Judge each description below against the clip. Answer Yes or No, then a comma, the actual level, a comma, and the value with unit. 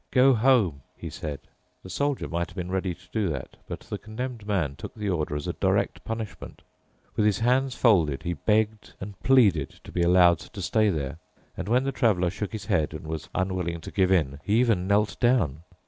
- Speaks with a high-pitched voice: No, very low, 95 Hz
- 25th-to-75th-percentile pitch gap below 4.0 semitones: No, average, 4.7 semitones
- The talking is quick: Yes, fast, 210 wpm